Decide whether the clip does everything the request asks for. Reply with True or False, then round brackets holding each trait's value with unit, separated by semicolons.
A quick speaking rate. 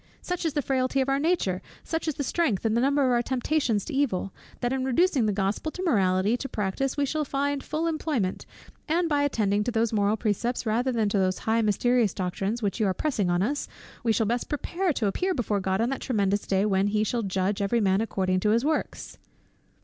True (220 wpm)